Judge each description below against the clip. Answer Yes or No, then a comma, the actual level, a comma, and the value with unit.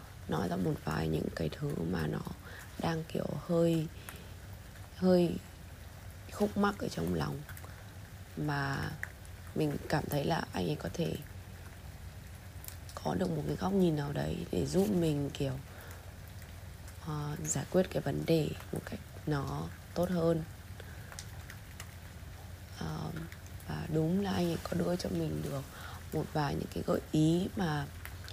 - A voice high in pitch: No, very low, 95 Hz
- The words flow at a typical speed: No, slow, 145 wpm